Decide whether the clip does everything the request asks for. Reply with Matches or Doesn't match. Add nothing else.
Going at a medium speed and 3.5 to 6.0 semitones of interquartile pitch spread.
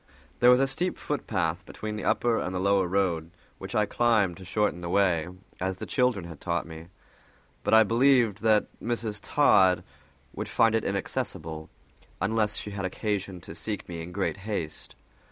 Matches